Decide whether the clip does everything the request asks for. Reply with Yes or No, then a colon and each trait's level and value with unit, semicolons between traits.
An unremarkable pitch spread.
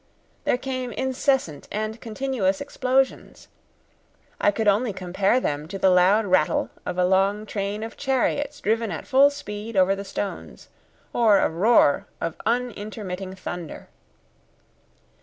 Yes: average, 4.6 semitones